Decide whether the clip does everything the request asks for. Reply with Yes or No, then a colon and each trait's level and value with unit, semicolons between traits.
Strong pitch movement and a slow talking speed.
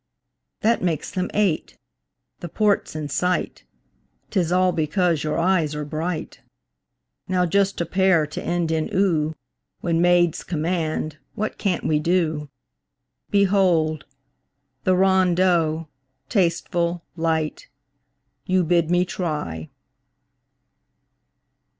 No: average, 2.8 semitones; slow, 105 wpm